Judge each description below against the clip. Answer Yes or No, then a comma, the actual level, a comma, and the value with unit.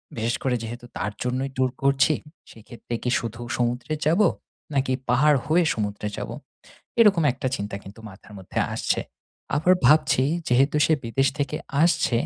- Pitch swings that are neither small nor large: Yes, average, 4.3 semitones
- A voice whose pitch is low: Yes, low, 130 Hz